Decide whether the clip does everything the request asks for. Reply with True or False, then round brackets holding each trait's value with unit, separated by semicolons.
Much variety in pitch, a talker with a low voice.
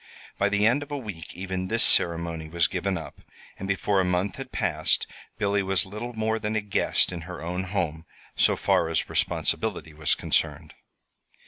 False (3.6 semitones; 95 Hz)